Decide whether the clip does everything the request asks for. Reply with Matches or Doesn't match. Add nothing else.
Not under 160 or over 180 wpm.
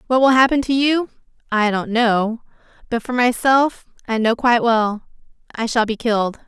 Matches